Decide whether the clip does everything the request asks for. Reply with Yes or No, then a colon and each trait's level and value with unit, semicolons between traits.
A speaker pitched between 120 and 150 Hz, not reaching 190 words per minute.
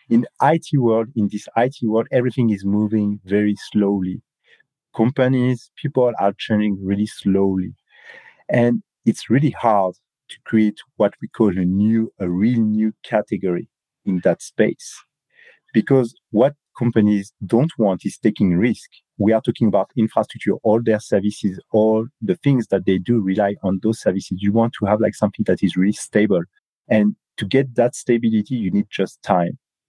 No: low, 110 Hz; average, 165 wpm